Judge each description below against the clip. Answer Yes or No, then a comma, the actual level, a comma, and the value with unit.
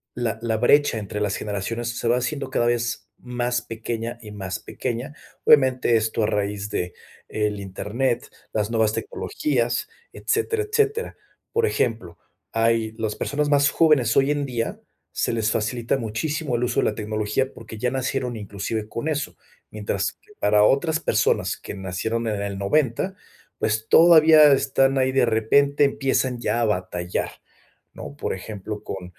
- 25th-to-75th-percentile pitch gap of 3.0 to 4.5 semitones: Yes, average, 4.1 semitones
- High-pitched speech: No, low, 115 Hz